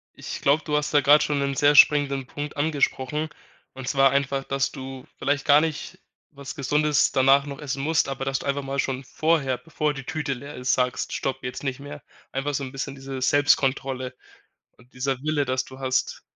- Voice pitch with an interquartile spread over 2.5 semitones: No, narrow, 1.7 semitones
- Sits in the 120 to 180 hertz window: Yes, medium, 140 Hz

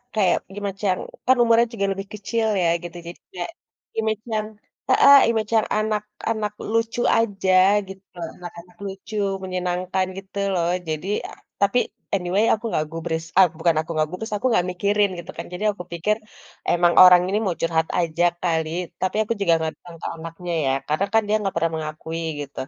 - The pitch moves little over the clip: No, average, 3.7 semitones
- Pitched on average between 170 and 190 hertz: Yes, medium, 185 Hz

